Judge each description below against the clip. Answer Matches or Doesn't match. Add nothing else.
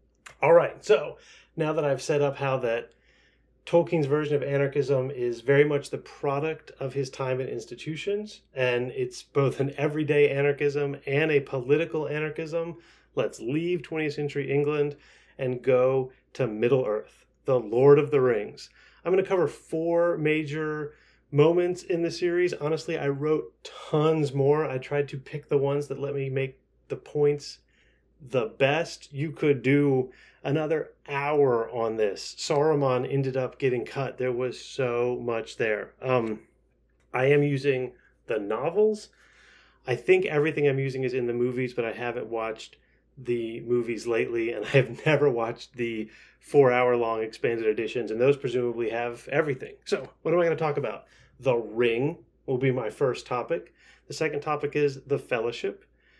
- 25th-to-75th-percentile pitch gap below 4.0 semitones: Matches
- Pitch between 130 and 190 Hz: Matches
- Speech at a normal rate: Matches